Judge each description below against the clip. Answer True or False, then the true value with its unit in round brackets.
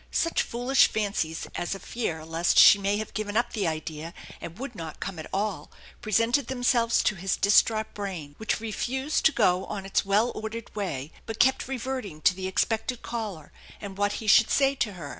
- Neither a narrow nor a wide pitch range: True (4.3 semitones)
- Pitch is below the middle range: False (210 Hz)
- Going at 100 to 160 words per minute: False (195 wpm)